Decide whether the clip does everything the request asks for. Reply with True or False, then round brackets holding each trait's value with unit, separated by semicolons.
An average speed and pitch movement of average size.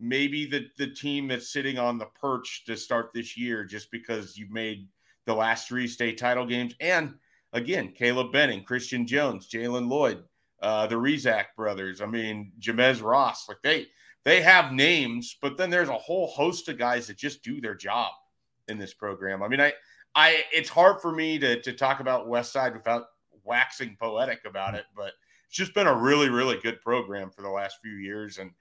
True (195 wpm; 3.8 semitones)